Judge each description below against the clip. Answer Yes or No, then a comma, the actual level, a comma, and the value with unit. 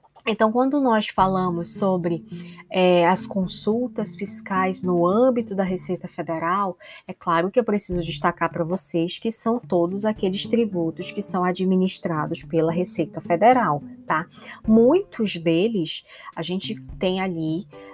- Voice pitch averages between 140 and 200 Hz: Yes, medium, 185 Hz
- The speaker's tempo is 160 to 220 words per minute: No, average, 135 wpm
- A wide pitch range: No, average, 3.8 semitones